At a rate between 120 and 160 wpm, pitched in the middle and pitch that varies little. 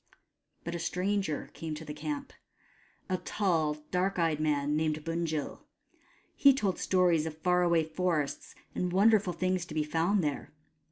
No: average, 155 wpm; medium, 170 Hz; average, 3.1 semitones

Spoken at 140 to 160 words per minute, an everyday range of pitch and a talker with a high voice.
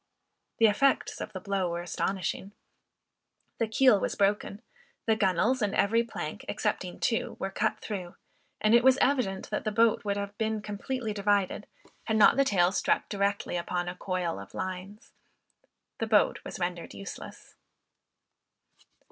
Yes: average, 155 wpm; average, 3.0 semitones; high, 205 Hz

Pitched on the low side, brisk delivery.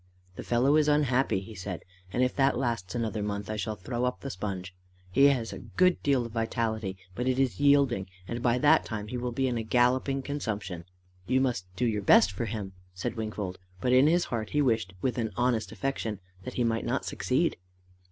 Yes: low, 120 Hz; fast, 210 wpm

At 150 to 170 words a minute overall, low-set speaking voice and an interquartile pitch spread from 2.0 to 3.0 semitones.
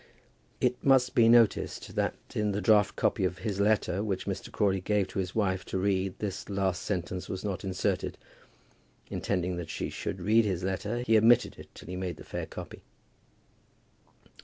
No: average, 180 wpm; low, 100 Hz; narrow, 2.5 semitones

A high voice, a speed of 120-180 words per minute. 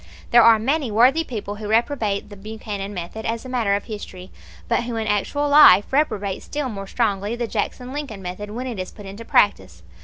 No: high, 220 Hz; fast, 205 wpm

